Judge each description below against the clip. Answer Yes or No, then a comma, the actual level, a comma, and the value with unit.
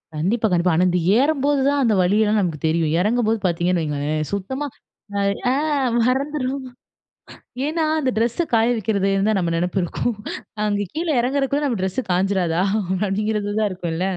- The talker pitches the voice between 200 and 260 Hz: Yes, high, 210 Hz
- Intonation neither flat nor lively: No, wide, 6.1 semitones